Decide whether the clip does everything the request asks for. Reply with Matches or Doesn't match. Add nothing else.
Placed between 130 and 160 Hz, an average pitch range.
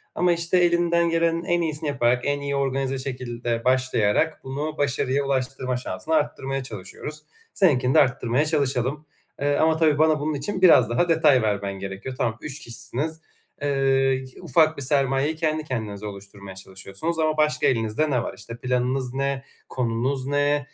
Matches